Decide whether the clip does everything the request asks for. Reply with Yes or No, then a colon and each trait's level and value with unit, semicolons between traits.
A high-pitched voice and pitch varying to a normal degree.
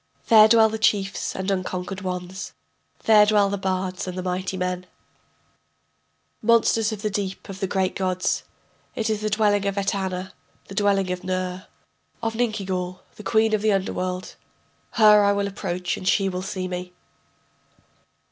No: high, 195 Hz; narrow, 2.3 semitones